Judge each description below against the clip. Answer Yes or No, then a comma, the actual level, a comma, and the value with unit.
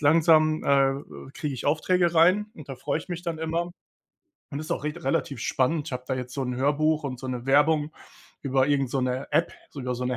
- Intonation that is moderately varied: Yes, average, 3.3 semitones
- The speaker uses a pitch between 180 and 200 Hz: No, medium, 145 Hz